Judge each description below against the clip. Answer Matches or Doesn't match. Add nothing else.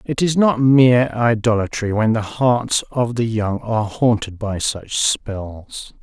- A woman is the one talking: Doesn't match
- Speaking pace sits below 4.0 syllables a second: Matches